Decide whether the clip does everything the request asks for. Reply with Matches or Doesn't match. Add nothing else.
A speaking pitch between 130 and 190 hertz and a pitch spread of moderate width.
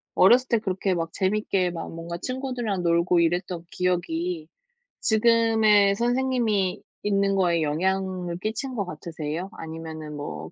Matches